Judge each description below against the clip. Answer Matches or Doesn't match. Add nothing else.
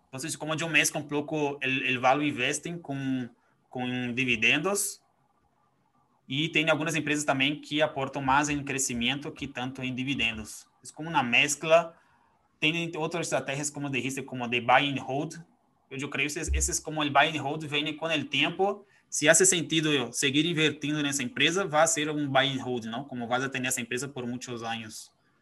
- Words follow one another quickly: Doesn't match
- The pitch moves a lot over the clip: Doesn't match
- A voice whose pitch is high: Doesn't match